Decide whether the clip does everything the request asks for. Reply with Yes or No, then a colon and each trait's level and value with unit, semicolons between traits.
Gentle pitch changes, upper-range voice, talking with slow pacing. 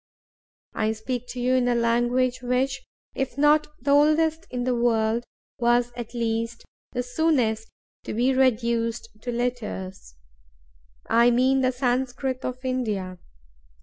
Yes: narrow, 2.2 semitones; high, 245 Hz; slow, 130 wpm